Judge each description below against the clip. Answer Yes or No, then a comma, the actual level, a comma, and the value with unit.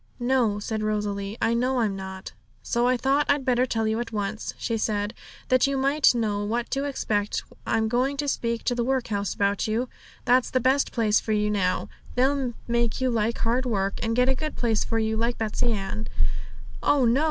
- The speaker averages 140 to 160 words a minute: No, average, 200 wpm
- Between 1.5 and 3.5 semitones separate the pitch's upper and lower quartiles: Yes, average, 3.2 semitones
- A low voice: No, high, 230 Hz